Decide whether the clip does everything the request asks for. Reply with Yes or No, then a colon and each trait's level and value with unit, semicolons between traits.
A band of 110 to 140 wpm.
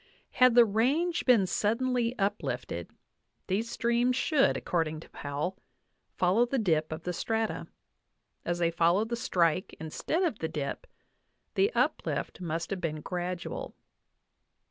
Yes: slow, 135 wpm